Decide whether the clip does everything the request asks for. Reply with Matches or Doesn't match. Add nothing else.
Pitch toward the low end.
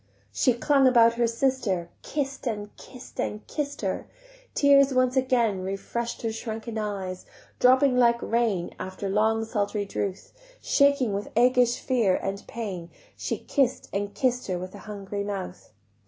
Doesn't match